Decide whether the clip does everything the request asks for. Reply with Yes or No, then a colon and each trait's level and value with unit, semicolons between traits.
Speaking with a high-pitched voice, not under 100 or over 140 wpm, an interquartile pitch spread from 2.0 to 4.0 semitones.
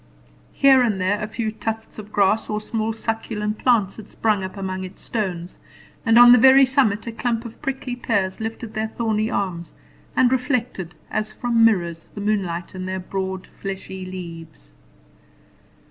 No: high, 215 Hz; average, 165 wpm; average, 3.4 semitones